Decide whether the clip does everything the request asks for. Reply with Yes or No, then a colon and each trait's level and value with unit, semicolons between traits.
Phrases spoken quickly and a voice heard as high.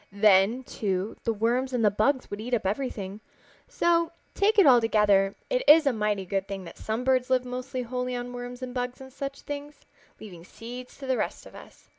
Yes: fast, 215 wpm; high, 245 Hz